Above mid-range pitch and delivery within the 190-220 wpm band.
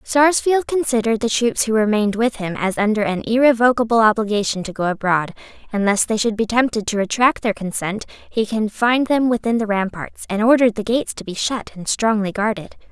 Yes: high, 220 Hz; average, 195 wpm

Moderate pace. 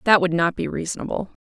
No: fast, 210 wpm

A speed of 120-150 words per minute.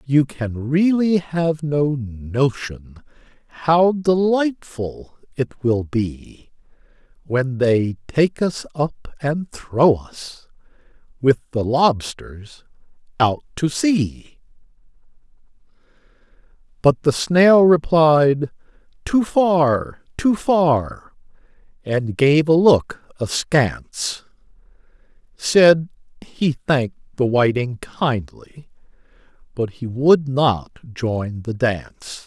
No: slow, 95 wpm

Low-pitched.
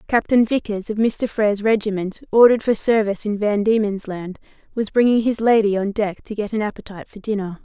No: high, 210 Hz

